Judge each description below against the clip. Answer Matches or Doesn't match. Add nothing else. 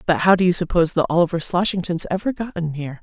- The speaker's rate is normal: Doesn't match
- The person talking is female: Matches